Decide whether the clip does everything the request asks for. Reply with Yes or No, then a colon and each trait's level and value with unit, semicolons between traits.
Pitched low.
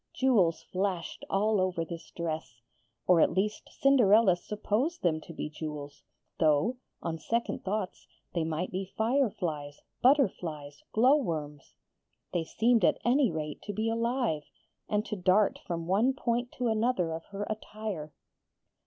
No: high, 190 Hz